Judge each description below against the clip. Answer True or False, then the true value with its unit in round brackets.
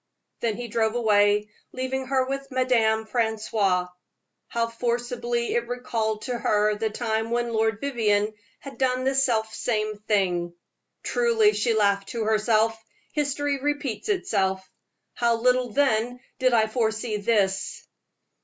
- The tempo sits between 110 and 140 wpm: True (135 wpm)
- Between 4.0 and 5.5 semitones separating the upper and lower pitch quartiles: False (2.9 semitones)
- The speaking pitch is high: True (230 Hz)